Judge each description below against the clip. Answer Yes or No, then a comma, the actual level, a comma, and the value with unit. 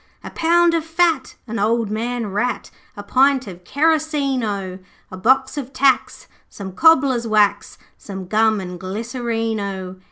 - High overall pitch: Yes, high, 230 Hz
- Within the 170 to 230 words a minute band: No, average, 150 wpm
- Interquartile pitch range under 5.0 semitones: No, average, 5.3 semitones